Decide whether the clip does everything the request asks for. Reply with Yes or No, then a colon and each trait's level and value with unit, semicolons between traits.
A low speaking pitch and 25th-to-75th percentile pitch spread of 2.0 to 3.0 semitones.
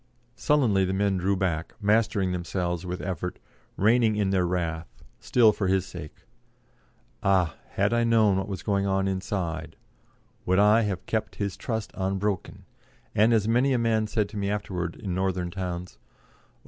Yes: very low, 95 Hz; average, 2.7 semitones